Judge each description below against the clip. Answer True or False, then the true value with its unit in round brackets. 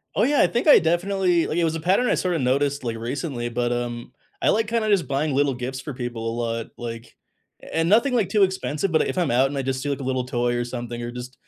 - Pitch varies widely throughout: True (6.4 semitones)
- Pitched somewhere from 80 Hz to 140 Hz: True (135 Hz)